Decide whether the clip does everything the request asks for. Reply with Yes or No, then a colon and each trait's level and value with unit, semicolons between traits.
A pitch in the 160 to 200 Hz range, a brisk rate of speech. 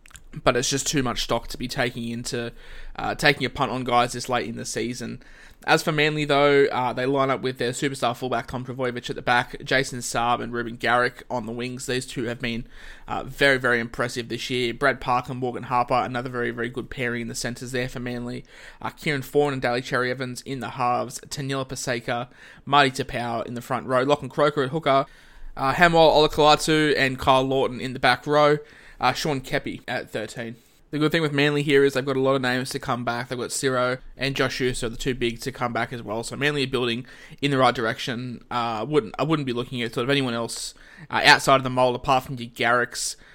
No: low, 125 Hz; fast, 230 wpm